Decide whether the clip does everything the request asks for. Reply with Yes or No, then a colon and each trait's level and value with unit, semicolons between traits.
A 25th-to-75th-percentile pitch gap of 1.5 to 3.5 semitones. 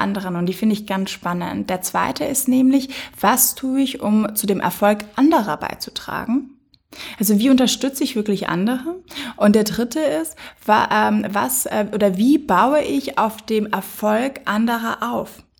No: average, 4.6 semitones